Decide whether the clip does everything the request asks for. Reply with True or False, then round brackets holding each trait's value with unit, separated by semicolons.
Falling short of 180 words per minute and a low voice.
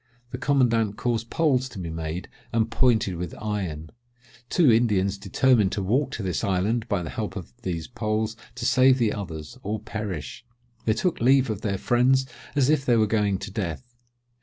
False (185 wpm; 110 Hz)